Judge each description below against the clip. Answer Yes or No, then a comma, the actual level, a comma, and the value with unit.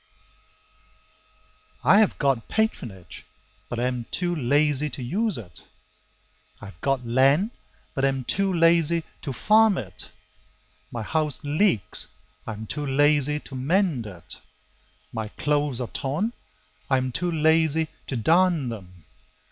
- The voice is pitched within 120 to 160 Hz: Yes, medium, 140 Hz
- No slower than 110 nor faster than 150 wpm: Yes, slow, 135 wpm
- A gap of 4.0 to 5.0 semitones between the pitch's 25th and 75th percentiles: No, wide, 5.6 semitones